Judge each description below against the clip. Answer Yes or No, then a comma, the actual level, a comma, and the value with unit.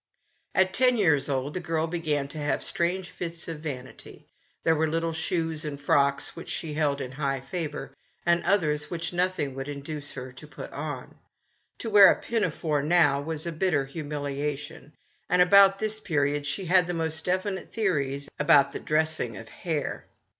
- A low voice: No, medium, 155 Hz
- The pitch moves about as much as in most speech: Yes, average, 3.4 semitones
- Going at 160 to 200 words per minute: Yes, average, 175 wpm